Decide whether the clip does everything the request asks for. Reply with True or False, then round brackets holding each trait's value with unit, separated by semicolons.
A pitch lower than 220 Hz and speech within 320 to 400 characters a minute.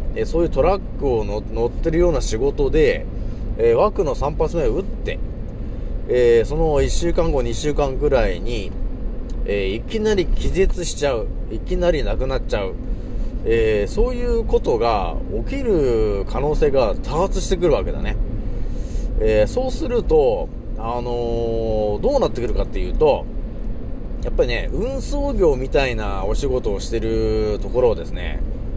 False (135 Hz; 300 characters per minute)